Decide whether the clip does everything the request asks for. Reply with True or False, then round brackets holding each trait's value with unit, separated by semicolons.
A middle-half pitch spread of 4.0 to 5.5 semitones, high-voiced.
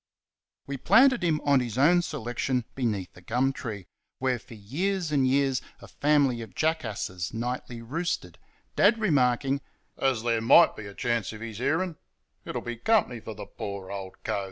False (5.1 semitones; 125 Hz)